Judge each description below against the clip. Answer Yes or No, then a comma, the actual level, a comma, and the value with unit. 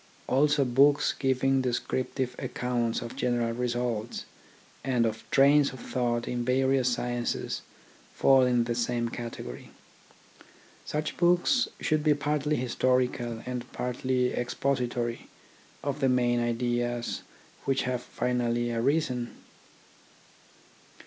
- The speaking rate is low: Yes, slow, 105 wpm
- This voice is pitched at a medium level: No, low, 125 Hz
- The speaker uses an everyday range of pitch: No, narrow, 2.0 semitones